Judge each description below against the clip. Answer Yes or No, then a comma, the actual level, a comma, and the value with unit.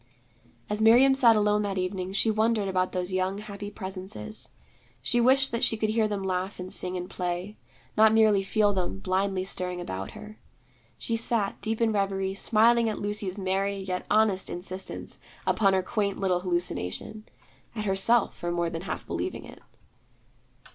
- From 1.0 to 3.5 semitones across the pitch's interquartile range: Yes, average, 2.7 semitones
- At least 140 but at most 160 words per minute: No, average, 170 wpm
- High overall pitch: Yes, high, 200 Hz